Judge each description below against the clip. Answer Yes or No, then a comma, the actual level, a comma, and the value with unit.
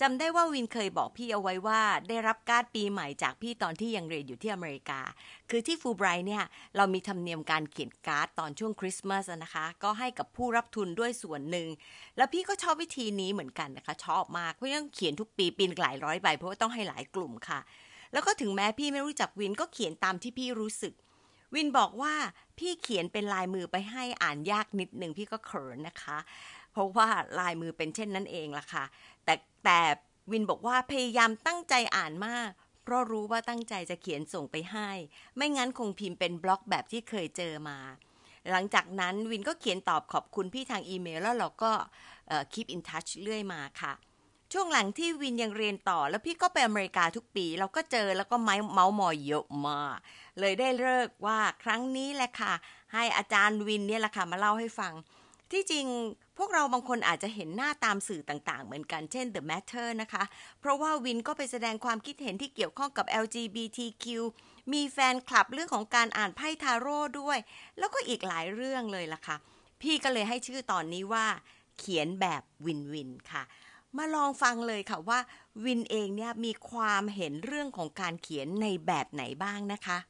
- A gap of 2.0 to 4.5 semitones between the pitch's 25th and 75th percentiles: No, average, 5.2 semitones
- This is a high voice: Yes, high, 215 Hz